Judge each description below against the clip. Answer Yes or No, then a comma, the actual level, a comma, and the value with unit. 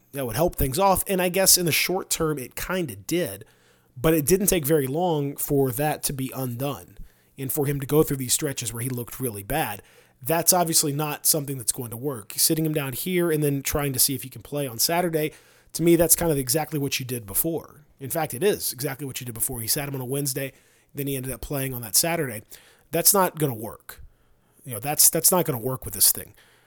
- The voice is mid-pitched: Yes, medium, 145 Hz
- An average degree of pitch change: Yes, average, 3.9 semitones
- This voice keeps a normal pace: No, fast, 245 wpm